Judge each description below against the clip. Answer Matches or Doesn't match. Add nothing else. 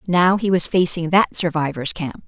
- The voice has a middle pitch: Matches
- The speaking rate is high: Doesn't match